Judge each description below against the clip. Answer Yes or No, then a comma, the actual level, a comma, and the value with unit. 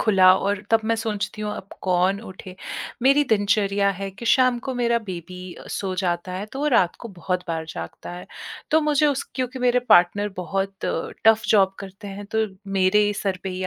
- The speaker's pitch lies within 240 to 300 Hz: No, high, 200 Hz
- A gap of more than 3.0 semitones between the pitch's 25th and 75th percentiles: Yes, average, 3.4 semitones